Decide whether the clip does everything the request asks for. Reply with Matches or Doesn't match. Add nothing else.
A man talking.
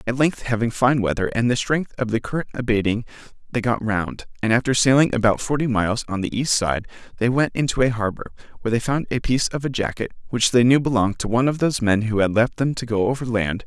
Matches